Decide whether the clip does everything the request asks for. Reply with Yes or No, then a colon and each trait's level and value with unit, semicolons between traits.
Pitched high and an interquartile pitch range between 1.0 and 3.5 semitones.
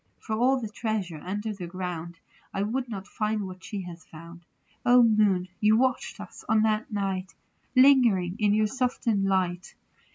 Yes: high, 205 Hz; average, 3.2 semitones